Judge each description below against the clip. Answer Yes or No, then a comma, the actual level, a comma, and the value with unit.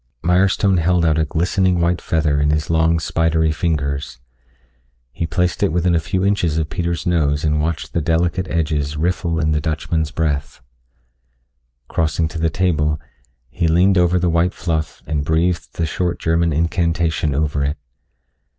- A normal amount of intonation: No, narrow, 2.1 semitones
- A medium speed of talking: Yes, average, 160 wpm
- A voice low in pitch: Yes, very low, 80 Hz